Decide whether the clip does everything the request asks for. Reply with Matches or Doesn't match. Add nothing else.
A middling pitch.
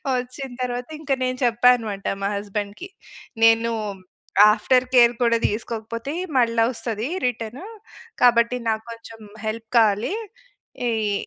Doesn't match